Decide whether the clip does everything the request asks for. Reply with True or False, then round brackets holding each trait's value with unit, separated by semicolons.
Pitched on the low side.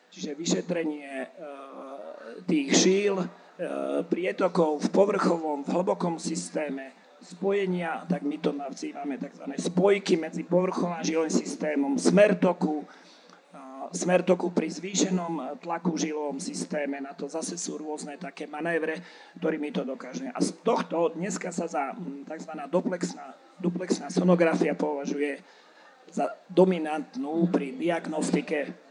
False (165 Hz)